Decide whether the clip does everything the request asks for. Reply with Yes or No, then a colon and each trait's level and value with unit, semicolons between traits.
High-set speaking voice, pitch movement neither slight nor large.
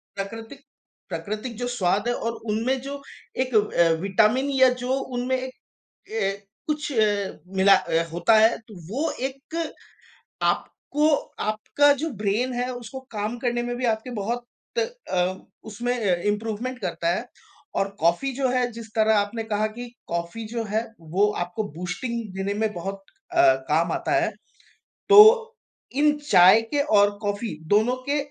Yes: high, 225 Hz; average, 4.0 semitones